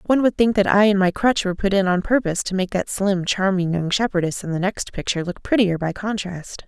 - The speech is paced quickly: Yes, fast, 250 wpm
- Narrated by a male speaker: No, female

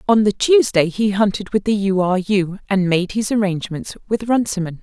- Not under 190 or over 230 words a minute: Yes, average, 200 wpm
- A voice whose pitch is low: No, high, 200 Hz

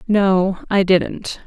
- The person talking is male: No, female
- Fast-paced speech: No, slow, 125 wpm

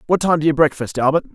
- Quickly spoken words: Yes, fast, 270 wpm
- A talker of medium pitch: Yes, medium, 150 Hz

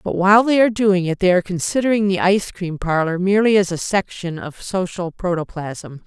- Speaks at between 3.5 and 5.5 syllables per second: No, 5.7 syllables/s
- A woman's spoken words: Yes, female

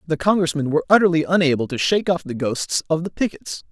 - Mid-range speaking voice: Yes, medium, 160 Hz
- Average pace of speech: No, fast, 210 wpm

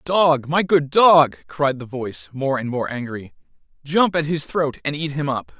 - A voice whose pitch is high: No, medium, 145 Hz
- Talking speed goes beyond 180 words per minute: Yes, fast, 205 wpm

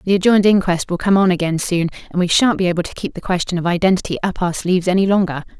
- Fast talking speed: Yes, fast, 255 wpm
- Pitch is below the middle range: No, medium, 180 Hz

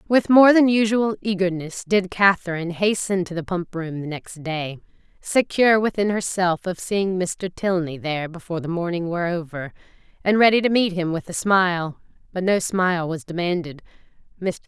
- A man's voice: No, female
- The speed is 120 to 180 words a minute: Yes, average, 170 wpm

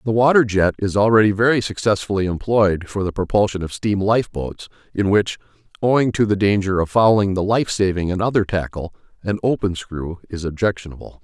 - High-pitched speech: No, low, 100 Hz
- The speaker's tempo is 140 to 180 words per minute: Yes, average, 175 wpm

